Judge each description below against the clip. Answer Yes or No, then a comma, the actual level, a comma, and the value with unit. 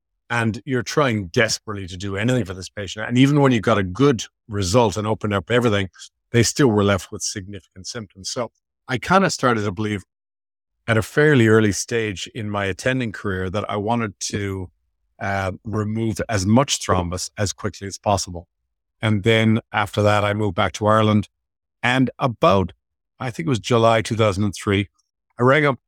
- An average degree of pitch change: Yes, average, 3.1 semitones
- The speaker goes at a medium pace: Yes, average, 180 wpm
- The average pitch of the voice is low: Yes, low, 105 Hz